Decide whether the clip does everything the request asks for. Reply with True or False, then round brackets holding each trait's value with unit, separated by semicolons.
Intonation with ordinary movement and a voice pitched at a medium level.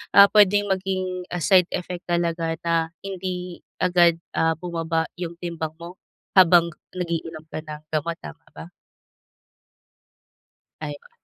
False (2.0 semitones; 170 Hz)